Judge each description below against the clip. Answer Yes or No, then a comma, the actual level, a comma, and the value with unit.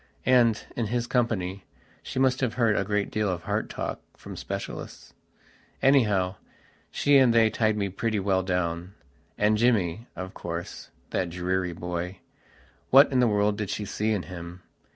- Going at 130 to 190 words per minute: Yes, average, 155 wpm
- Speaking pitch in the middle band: No, low, 105 Hz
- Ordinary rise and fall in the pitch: Yes, average, 4.2 semitones